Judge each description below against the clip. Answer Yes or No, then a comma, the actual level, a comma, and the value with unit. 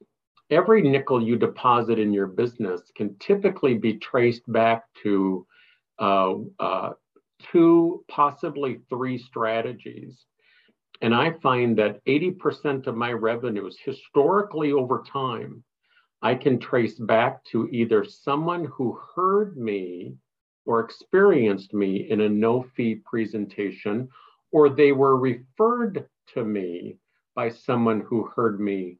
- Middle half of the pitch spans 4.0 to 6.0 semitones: Yes, average, 5.0 semitones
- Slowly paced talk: Yes, slow, 120 wpm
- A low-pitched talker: Yes, low, 120 Hz